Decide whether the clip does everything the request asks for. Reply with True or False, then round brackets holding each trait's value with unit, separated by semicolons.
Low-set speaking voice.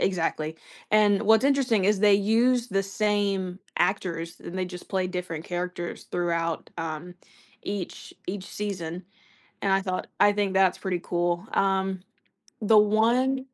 False (190 Hz)